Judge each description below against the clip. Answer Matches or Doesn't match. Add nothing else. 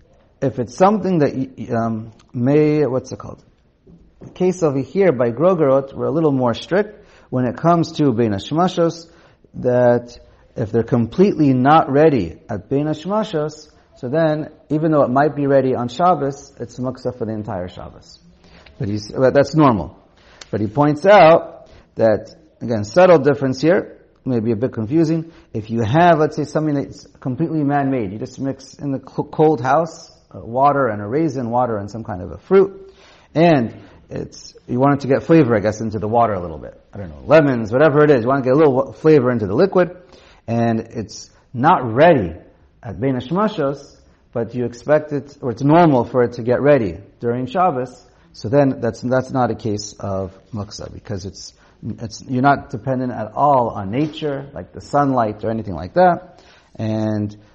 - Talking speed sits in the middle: Matches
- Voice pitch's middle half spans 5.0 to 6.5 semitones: Matches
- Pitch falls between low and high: Doesn't match